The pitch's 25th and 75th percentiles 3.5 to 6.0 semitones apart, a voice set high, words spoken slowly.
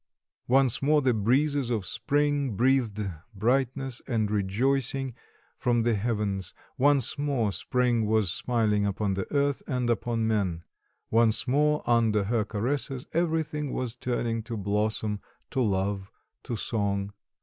No: average, 4.2 semitones; low, 115 Hz; slow, 130 wpm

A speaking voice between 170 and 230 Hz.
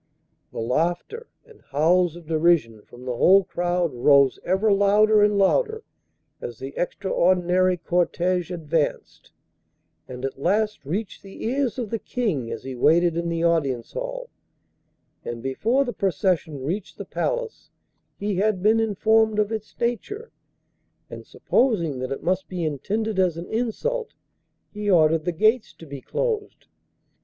Yes: medium, 185 Hz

